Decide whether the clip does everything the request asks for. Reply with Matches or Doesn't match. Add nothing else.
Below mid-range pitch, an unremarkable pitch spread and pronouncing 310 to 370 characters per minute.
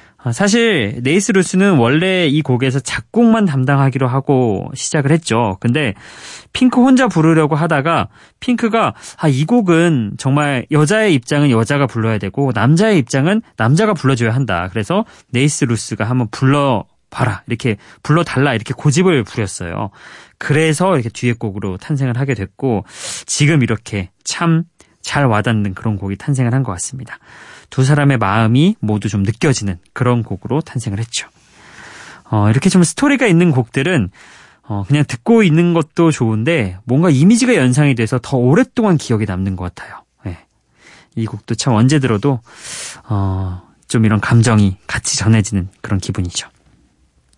Doesn't match